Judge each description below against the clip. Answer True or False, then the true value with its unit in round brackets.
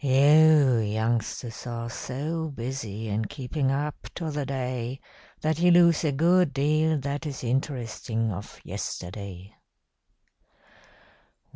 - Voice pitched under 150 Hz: True (135 Hz)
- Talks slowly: True (115 wpm)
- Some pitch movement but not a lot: True (4.8 semitones)